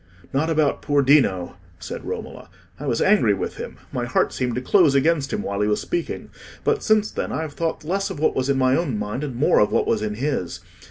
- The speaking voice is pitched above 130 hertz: Yes, medium, 140 Hz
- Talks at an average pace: No, fast, 235 wpm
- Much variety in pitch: Yes, wide, 5.8 semitones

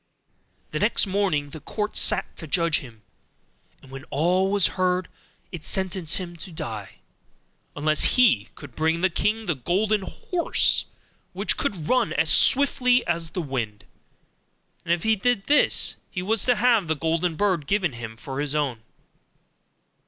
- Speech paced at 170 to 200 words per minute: No, average, 160 wpm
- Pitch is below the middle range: No, medium, 175 Hz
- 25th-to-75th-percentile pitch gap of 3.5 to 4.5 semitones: No, wide, 5.6 semitones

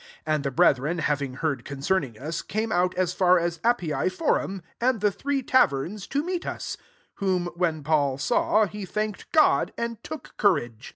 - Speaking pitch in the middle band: Yes, medium, 180 Hz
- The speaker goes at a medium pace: Yes, average, 180 wpm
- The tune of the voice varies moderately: No, wide, 6.3 semitones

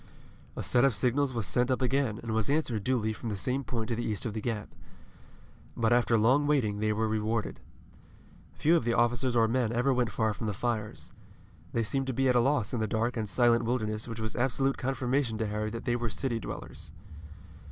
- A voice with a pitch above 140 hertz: No, low, 115 Hz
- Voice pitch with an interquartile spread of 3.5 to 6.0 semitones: No, average, 2.7 semitones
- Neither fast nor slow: No, fast, 220 wpm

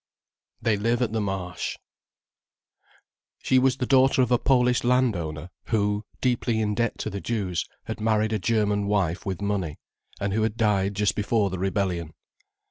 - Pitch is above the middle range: No, low, 105 Hz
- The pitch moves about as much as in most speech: Yes, average, 3.3 semitones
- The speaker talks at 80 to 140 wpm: No, average, 165 wpm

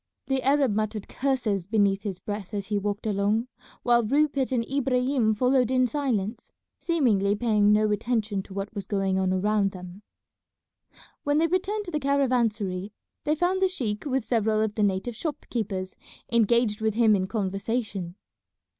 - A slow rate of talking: No, average, 165 wpm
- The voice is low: No, high, 220 Hz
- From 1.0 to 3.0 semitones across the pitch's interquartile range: No, average, 4.2 semitones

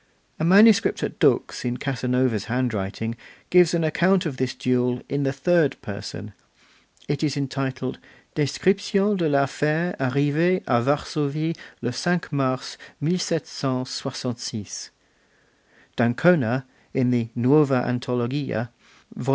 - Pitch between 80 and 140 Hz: Yes, low, 135 Hz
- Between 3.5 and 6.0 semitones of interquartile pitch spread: Yes, average, 4.2 semitones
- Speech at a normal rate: No, slow, 110 wpm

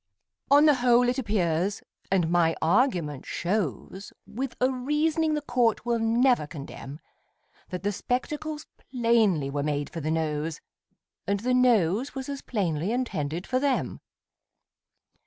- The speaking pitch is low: No, high, 220 Hz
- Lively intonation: Yes, wide, 7.6 semitones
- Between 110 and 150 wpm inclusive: Yes, average, 140 wpm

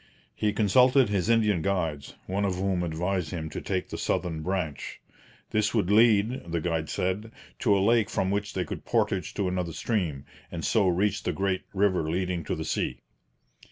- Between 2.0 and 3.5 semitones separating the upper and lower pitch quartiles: Yes, average, 3.1 semitones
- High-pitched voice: No, very low, 95 Hz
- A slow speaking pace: No, average, 185 wpm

